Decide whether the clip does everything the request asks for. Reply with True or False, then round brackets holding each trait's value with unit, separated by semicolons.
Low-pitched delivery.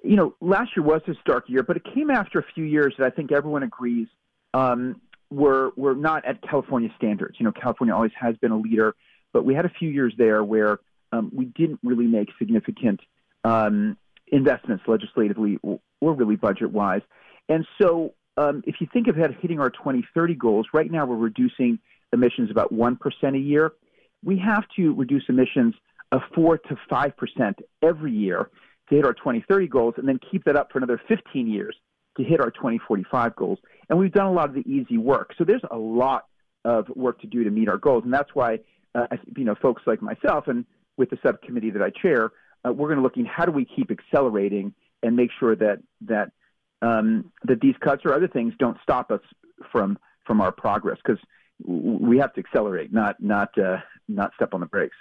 False (155 Hz)